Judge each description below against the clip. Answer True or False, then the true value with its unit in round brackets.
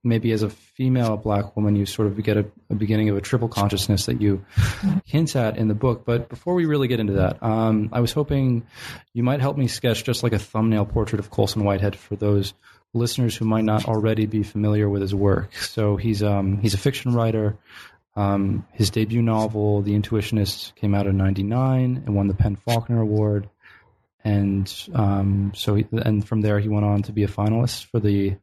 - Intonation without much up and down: True (2.2 semitones)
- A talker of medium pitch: False (110 Hz)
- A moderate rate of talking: False (210 wpm)